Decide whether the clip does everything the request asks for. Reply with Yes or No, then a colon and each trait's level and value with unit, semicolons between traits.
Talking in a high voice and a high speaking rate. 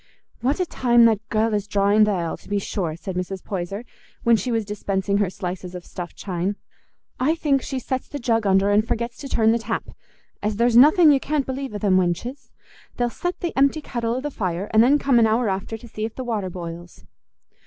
Yes: high, 220 Hz; fast, 225 wpm